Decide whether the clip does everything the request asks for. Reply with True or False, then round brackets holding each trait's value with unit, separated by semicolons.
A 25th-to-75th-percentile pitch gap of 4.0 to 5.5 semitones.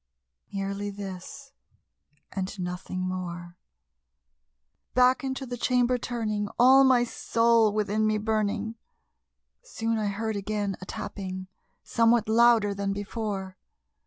False (3.1 semitones)